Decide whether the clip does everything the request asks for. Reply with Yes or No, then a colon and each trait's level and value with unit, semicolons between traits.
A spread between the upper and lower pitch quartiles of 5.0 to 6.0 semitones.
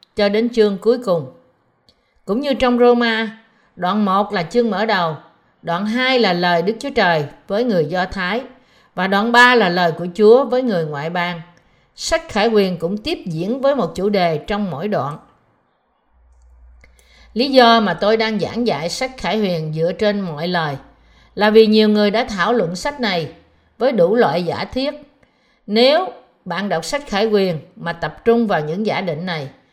Yes: wide, 5.6 semitones